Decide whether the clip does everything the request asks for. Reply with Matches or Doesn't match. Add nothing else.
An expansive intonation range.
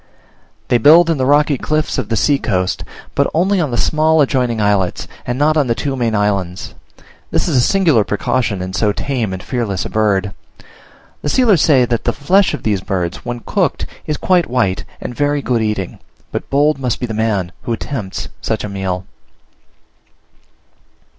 Matches